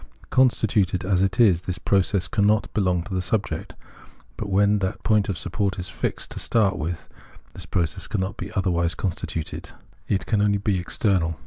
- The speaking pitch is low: Yes, very low, 95 Hz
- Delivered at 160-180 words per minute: Yes, average, 175 wpm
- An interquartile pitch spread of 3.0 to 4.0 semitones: No, narrow, 2.4 semitones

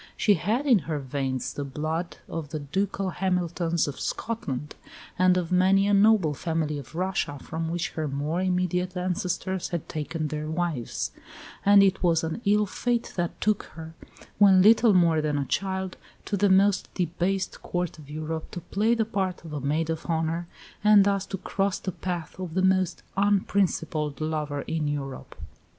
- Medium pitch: Yes, medium, 175 Hz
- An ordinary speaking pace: Yes, average, 170 wpm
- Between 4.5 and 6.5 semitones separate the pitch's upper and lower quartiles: No, average, 3.7 semitones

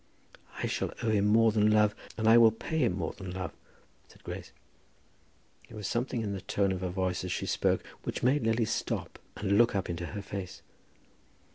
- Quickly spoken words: Yes, fast, 210 wpm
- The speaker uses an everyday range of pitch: Yes, average, 3.1 semitones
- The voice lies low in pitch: Yes, low, 105 Hz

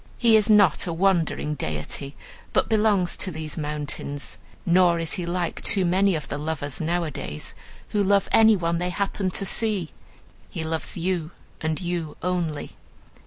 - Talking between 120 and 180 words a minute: Yes, average, 160 wpm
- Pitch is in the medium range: Yes, medium, 170 Hz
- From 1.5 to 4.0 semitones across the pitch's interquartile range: Yes, average, 3.7 semitones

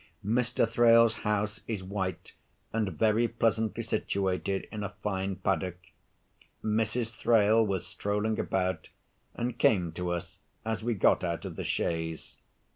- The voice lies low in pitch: Yes, low, 105 Hz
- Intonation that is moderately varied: Yes, average, 3.1 semitones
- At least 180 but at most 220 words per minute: No, slow, 135 wpm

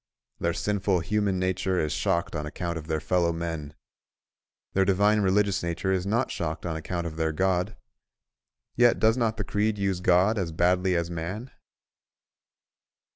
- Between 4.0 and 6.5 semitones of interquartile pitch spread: No, average, 3.2 semitones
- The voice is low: Yes, very low, 90 Hz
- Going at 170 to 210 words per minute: No, average, 160 wpm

